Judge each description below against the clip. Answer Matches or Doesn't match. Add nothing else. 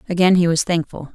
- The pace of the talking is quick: Matches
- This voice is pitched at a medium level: Matches